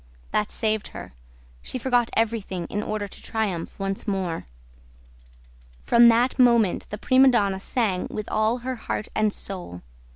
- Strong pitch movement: No, average, 3.3 semitones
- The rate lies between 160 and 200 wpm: No, average, 150 wpm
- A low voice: No, high, 215 Hz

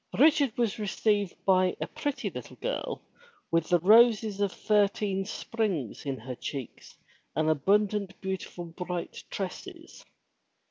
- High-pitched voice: Yes, high, 200 Hz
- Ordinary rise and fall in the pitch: Yes, average, 3.8 semitones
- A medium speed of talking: No, slow, 125 wpm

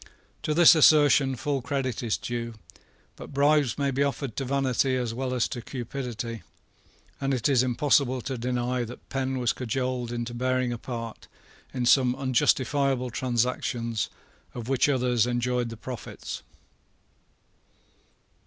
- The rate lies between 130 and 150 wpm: Yes, average, 140 wpm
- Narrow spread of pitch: Yes, narrow, 2.1 semitones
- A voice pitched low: Yes, low, 125 Hz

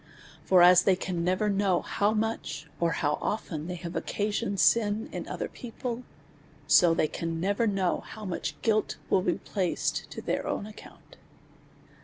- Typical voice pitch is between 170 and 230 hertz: Yes, high, 190 Hz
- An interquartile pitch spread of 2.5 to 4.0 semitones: Yes, average, 3.5 semitones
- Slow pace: No, average, 165 wpm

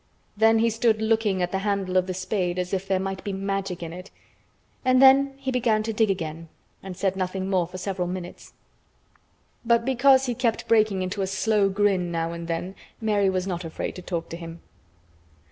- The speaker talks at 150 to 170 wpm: No, average, 195 wpm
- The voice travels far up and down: No, average, 3.4 semitones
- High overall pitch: Yes, high, 195 Hz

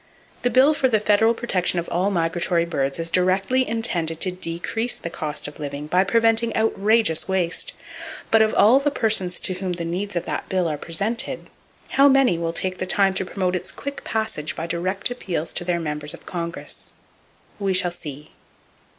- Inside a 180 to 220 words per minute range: Yes, average, 185 wpm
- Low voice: No, medium, 185 Hz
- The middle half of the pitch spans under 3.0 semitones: No, average, 4.7 semitones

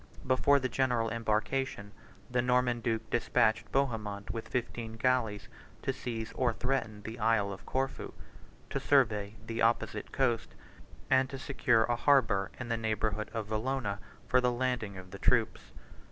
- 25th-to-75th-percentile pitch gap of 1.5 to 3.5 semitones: Yes, average, 2.9 semitones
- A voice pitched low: Yes, low, 115 Hz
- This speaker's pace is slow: No, average, 155 wpm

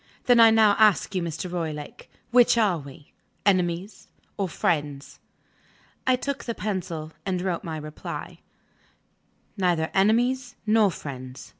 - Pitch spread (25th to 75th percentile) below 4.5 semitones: No, wide, 5.4 semitones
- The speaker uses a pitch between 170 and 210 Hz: Yes, medium, 185 Hz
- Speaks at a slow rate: Yes, slow, 130 wpm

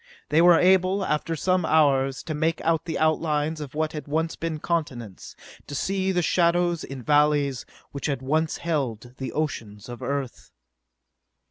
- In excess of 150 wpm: Yes, average, 160 wpm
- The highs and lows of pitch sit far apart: No, average, 3.3 semitones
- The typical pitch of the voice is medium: Yes, medium, 155 Hz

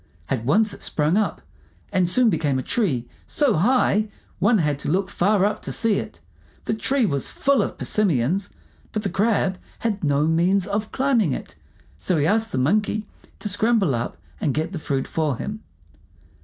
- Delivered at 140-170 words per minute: No, average, 185 wpm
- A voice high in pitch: Yes, high, 195 Hz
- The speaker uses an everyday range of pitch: No, wide, 6.2 semitones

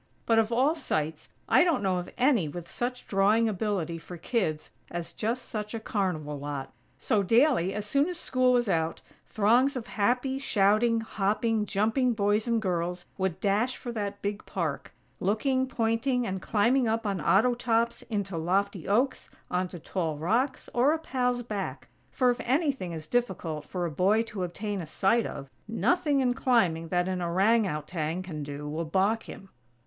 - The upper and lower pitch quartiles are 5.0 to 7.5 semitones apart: Yes, average, 5.3 semitones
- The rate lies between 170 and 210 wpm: Yes, average, 175 wpm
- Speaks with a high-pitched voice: Yes, high, 210 Hz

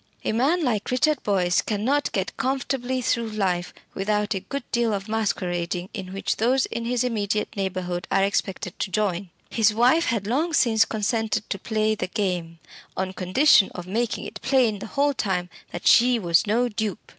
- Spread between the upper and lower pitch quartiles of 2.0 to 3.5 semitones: No, average, 4.1 semitones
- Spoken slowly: No, average, 180 wpm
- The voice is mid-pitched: No, high, 215 Hz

